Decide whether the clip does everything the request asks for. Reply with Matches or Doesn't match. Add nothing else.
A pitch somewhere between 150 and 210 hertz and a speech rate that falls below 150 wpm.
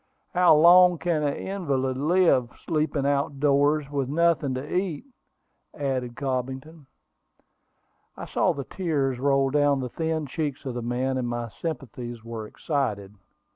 Doesn't match